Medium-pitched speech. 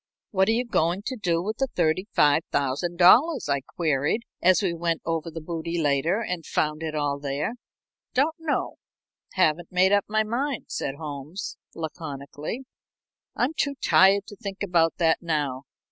Yes: medium, 170 Hz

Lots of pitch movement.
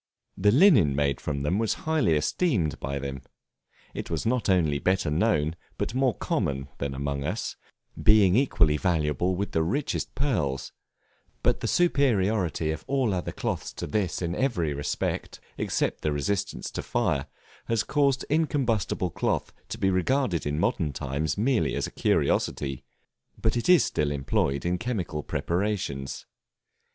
Yes: wide, 7.6 semitones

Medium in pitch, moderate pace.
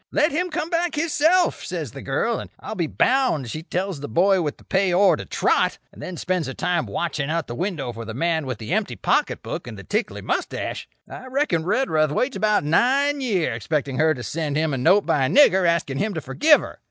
No: medium, 175 Hz; fast, 230 wpm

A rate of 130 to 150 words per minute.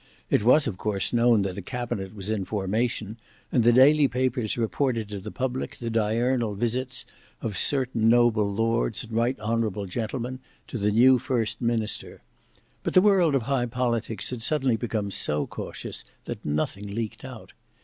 No: average, 170 wpm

